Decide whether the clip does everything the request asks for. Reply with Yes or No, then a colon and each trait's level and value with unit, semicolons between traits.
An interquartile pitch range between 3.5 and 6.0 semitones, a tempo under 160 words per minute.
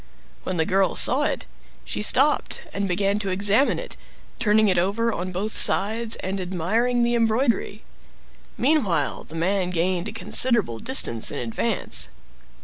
Yes: average, 4.1 semitones; average, 145 wpm